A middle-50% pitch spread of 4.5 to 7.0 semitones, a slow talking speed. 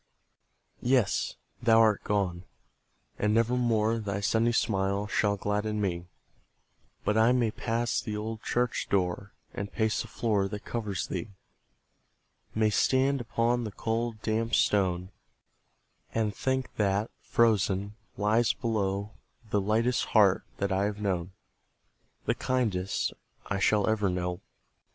No: narrow, 2.6 semitones; slow, 130 wpm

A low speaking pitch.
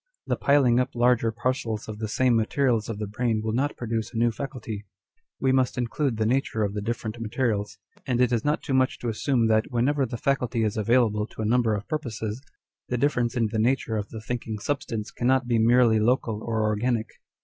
Yes: low, 115 Hz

